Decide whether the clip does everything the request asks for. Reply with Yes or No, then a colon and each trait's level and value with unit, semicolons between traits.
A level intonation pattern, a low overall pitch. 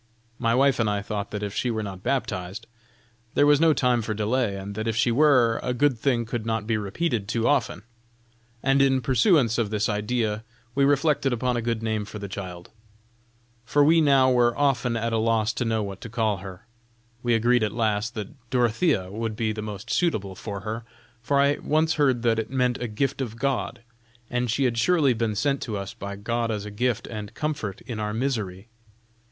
No: average, 3.5 semitones; low, 115 Hz